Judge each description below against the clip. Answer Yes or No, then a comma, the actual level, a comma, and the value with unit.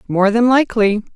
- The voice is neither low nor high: No, high, 220 Hz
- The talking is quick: No, average, 155 wpm